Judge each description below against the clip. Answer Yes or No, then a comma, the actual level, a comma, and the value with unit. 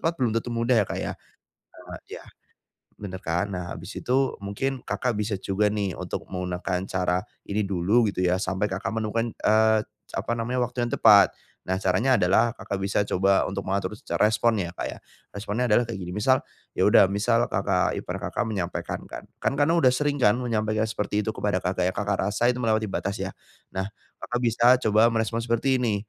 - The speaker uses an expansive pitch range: No, average, 3.5 semitones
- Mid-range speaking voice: No, low, 105 Hz